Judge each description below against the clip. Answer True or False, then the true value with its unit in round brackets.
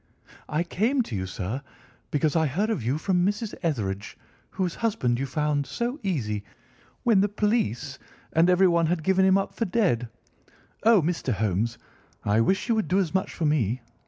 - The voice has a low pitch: False (165 Hz)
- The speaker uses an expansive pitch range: True (8.0 semitones)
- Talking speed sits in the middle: True (180 wpm)